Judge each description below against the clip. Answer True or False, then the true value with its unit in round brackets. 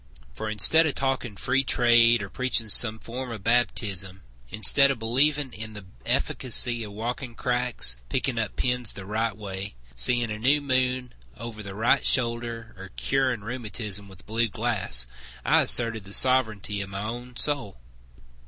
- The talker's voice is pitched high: False (115 Hz)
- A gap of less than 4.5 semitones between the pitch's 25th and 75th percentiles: True (3.3 semitones)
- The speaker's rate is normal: True (160 wpm)